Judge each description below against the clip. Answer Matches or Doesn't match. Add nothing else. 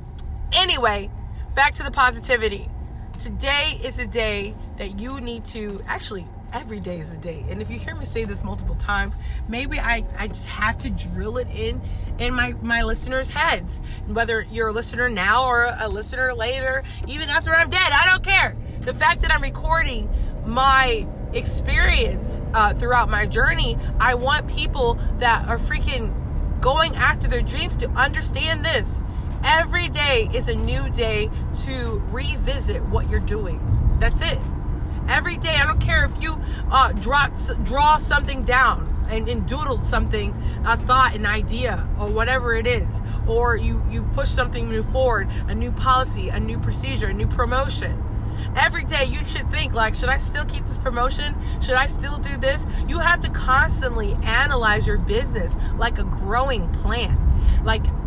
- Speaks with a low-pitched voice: Matches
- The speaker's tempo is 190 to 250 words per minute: Doesn't match